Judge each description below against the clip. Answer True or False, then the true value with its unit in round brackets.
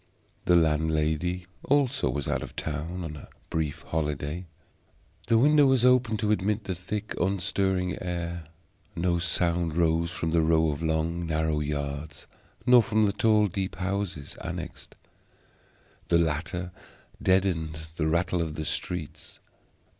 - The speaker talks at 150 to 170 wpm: False (140 wpm)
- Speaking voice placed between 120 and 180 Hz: False (85 Hz)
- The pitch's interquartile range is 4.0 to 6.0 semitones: False (3.5 semitones)